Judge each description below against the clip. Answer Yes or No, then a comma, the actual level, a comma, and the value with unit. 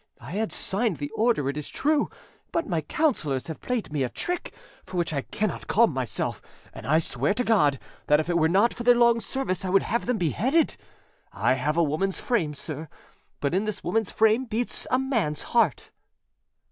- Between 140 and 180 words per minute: No, average, 200 wpm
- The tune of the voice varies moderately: No, wide, 7.7 semitones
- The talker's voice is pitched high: Yes, high, 195 Hz